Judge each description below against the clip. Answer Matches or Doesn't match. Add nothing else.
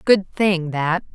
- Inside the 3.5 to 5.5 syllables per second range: Doesn't match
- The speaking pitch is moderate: Matches